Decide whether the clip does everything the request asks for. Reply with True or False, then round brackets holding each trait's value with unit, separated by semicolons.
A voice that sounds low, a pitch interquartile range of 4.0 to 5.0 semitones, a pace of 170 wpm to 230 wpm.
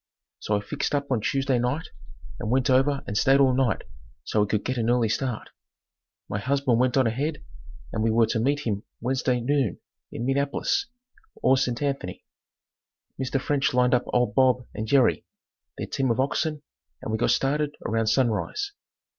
False (130 Hz; 3.3 semitones; 180 wpm)